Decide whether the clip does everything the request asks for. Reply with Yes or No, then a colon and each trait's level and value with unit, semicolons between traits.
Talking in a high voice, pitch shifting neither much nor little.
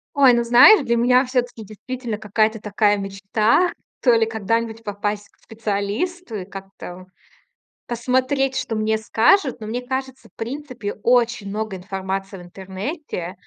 Yes: high, 225 Hz; average, 3.6 semitones